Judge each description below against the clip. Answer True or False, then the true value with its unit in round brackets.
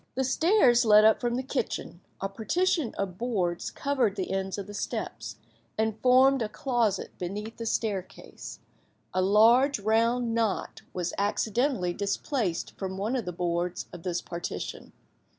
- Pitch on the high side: True (215 Hz)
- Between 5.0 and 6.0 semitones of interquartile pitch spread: False (4.3 semitones)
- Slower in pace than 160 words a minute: True (150 wpm)